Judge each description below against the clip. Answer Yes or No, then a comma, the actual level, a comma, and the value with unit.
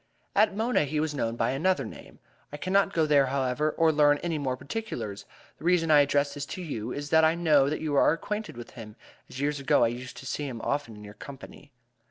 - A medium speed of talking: No, fast, 235 wpm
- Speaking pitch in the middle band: Yes, medium, 145 Hz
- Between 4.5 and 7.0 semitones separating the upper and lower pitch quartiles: No, average, 3.4 semitones